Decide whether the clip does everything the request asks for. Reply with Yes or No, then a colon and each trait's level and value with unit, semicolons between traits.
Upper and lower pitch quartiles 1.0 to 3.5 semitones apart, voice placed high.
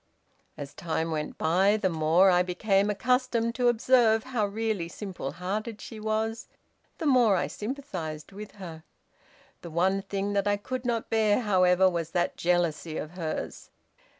No: average, 4.2 semitones; high, 195 Hz